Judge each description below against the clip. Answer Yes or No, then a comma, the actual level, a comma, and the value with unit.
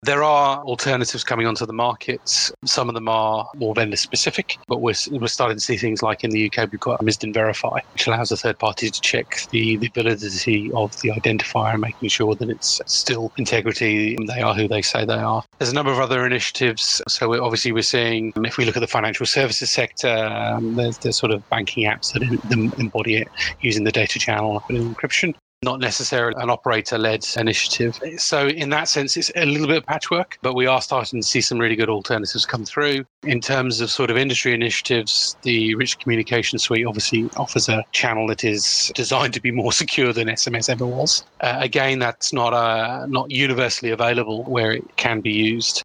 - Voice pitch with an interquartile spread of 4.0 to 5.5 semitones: No, narrow, 2.4 semitones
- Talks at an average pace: No, fast, 210 wpm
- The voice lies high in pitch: No, low, 115 Hz